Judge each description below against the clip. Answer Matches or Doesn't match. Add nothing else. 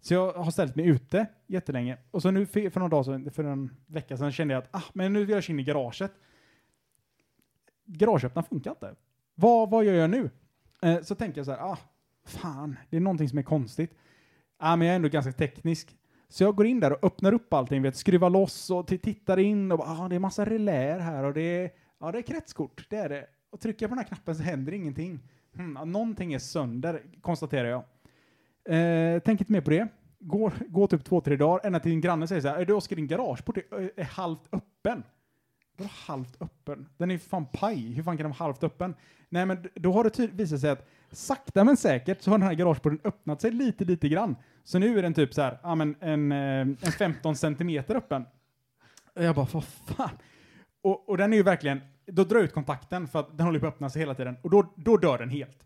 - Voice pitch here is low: Doesn't match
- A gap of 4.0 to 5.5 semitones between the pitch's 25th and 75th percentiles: Matches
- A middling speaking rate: Doesn't match